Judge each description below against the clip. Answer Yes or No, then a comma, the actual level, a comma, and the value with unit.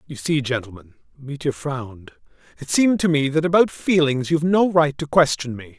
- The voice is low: No, medium, 145 Hz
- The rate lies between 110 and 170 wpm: Yes, average, 165 wpm